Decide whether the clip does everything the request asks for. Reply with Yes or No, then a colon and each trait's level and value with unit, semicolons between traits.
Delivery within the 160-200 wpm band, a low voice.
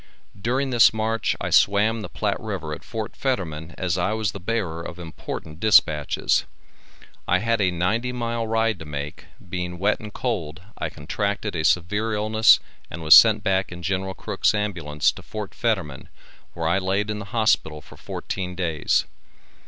Yes: average, 170 wpm; very low, 95 Hz